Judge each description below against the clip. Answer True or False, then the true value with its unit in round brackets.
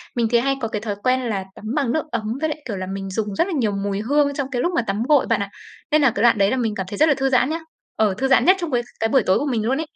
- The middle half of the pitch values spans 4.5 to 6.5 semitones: True (5.1 semitones)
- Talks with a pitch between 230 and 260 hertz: True (240 Hz)